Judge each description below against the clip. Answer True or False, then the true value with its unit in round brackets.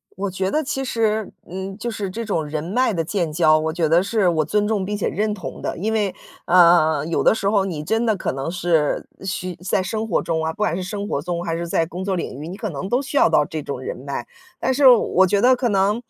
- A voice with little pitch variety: False (4.4 semitones)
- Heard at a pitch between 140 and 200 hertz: True (190 Hz)